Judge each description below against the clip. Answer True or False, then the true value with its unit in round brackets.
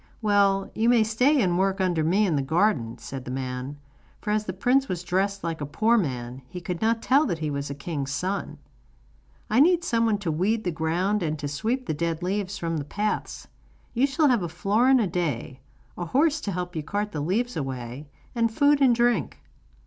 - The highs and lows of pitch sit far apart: True (6.3 semitones)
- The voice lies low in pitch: False (190 Hz)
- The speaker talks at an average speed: False (215 wpm)